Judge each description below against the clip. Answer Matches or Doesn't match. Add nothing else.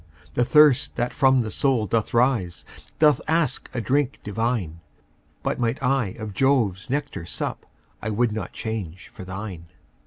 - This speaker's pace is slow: Doesn't match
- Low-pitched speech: Matches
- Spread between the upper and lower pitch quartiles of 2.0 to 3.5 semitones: Doesn't match